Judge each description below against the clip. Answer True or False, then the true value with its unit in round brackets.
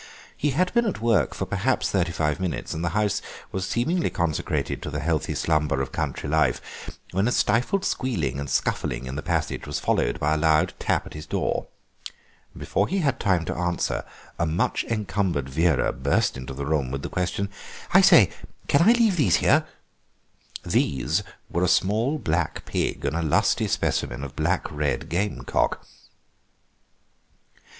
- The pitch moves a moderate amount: False (6.4 semitones)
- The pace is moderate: True (170 wpm)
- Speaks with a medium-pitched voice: False (85 Hz)